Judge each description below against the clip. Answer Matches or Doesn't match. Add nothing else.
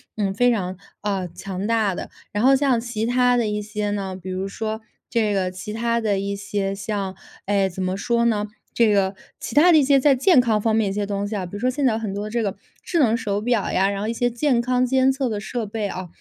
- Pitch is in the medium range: Doesn't match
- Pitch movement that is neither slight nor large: Matches